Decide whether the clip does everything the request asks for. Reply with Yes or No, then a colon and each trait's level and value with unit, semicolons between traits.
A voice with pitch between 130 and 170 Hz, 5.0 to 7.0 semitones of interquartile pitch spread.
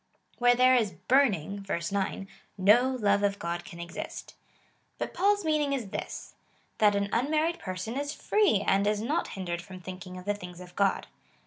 No: high, 205 Hz; wide, 5.6 semitones